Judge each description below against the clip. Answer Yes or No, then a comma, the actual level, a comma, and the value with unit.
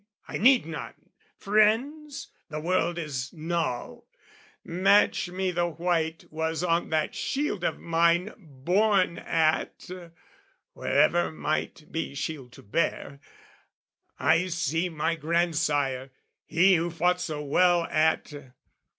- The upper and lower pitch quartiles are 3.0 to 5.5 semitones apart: No, narrow, 2.6 semitones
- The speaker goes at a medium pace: No, slow, 110 wpm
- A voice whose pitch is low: No, medium, 170 Hz